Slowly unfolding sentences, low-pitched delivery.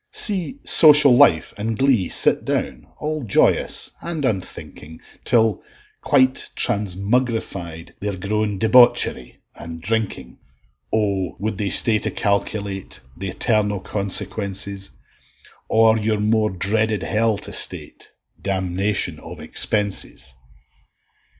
Yes: slow, 105 wpm; low, 105 Hz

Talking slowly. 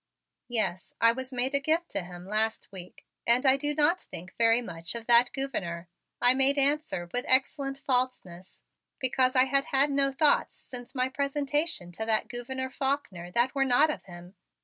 No: average, 180 wpm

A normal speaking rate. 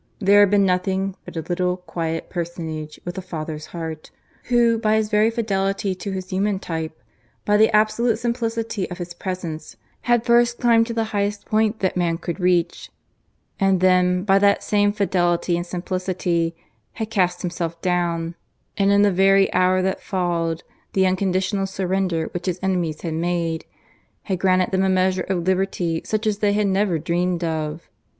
Yes: average, 170 wpm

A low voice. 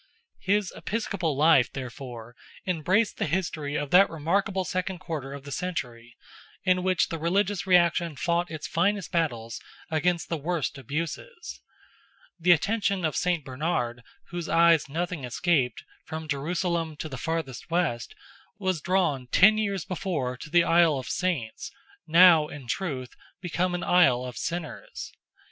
No: medium, 165 Hz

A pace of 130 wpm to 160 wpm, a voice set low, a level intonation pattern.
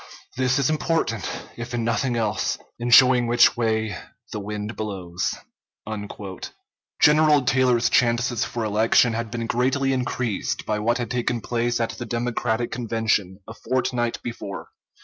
Yes: average, 140 wpm; low, 120 Hz; narrow, 2.0 semitones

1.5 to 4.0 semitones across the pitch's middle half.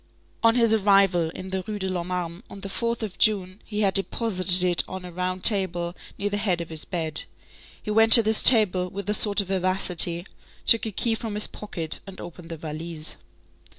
Yes: average, 3.1 semitones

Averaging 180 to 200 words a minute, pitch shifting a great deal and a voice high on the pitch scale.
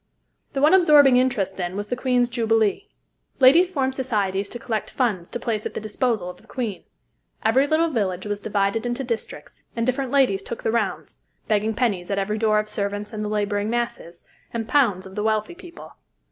No: average, 195 wpm; average, 3.9 semitones; high, 225 Hz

